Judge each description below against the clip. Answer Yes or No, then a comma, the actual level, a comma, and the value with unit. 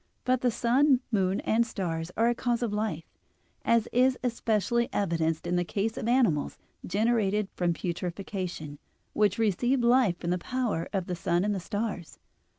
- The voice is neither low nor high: No, high, 210 Hz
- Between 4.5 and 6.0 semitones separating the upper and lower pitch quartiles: Yes, average, 5.1 semitones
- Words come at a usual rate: Yes, average, 160 wpm